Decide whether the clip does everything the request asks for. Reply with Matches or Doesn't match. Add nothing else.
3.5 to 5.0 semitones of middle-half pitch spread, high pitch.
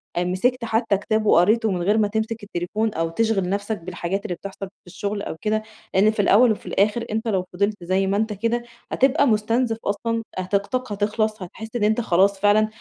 Doesn't match